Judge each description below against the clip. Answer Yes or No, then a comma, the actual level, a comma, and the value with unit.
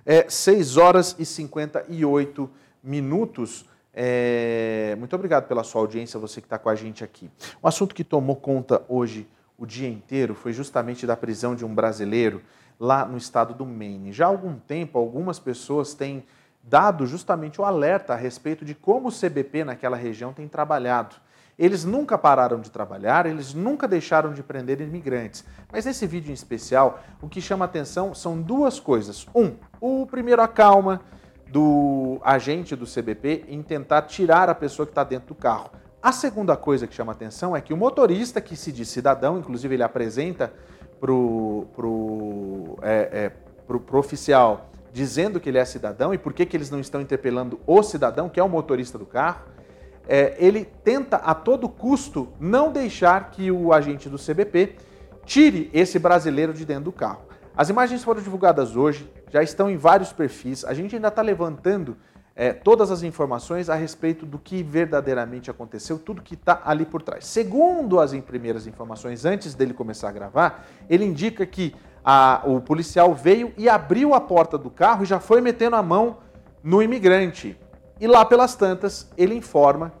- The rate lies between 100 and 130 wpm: No, average, 180 wpm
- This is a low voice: No, medium, 150 Hz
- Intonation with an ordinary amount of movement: No, wide, 6.7 semitones